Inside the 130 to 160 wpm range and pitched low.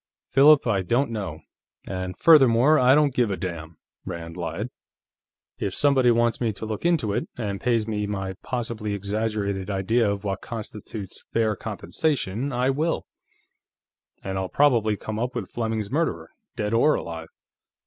Yes: average, 155 wpm; low, 110 Hz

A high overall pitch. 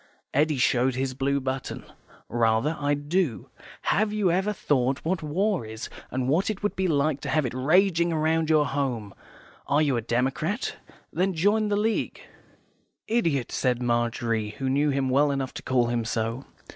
No: medium, 140 Hz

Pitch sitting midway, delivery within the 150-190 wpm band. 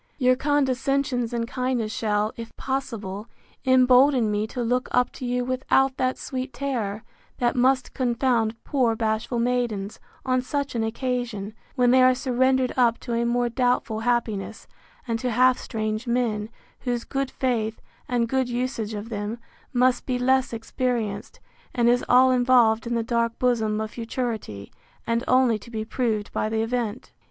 No: high, 245 Hz; average, 160 wpm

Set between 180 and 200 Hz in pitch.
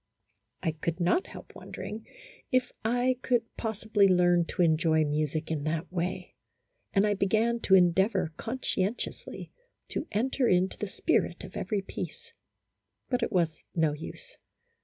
Yes: high, 190 Hz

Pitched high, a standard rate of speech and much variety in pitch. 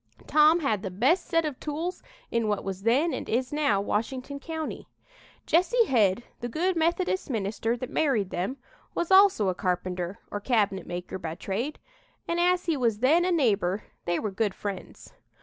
Yes: high, 240 Hz; average, 175 wpm; wide, 8.2 semitones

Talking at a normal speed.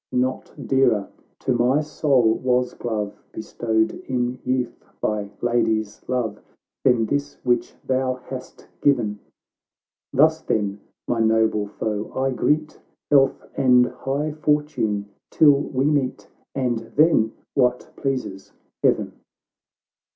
No: slow, 115 wpm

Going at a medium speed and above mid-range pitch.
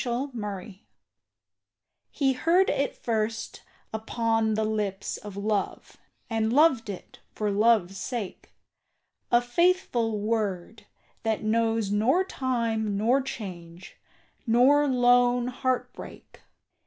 No: slow, 105 wpm; high, 225 Hz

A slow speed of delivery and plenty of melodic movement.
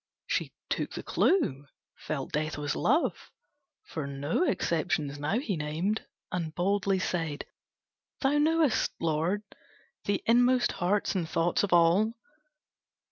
Yes: slow, 125 wpm; wide, 5.9 semitones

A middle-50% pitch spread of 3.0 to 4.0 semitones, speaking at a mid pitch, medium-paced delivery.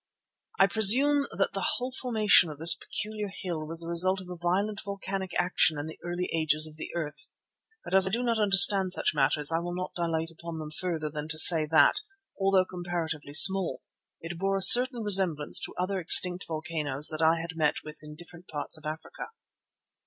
Yes: average, 3.6 semitones; medium, 175 Hz; average, 195 wpm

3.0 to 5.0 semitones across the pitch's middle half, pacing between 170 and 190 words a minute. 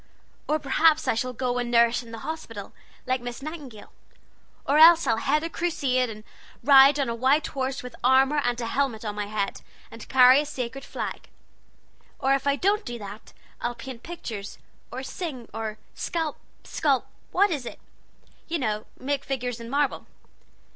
Yes: average, 3.7 semitones; average, 175 wpm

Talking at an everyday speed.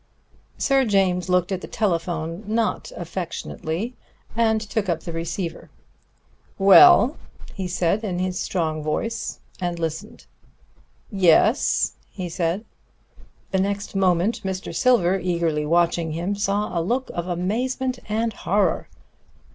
No: slow, 125 wpm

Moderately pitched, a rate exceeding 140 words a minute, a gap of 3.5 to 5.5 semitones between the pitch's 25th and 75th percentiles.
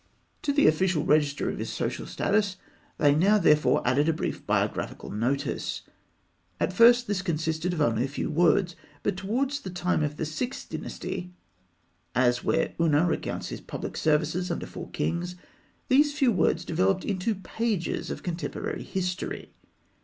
Yes: medium, 175 Hz; average, 155 wpm; average, 4.4 semitones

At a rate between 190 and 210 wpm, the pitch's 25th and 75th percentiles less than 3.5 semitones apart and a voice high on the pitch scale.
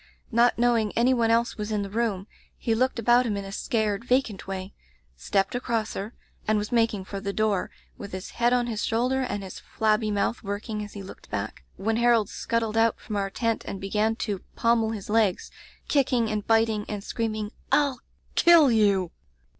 Yes: average, 195 wpm; narrow, 2.5 semitones; high, 220 Hz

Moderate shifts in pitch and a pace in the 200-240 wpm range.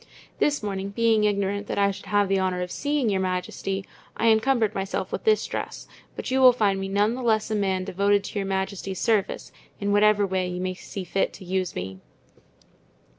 No: narrow, 2.2 semitones; fast, 205 wpm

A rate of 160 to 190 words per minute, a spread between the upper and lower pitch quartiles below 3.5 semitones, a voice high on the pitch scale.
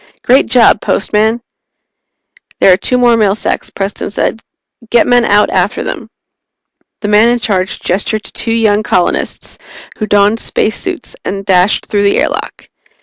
No: average, 150 wpm; narrow, 2.4 semitones; high, 215 Hz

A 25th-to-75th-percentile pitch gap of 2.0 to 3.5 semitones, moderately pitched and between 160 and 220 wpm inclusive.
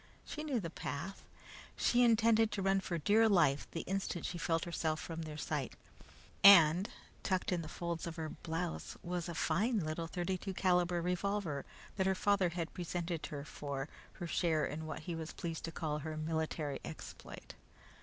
Yes: average, 3.2 semitones; medium, 170 Hz; average, 175 wpm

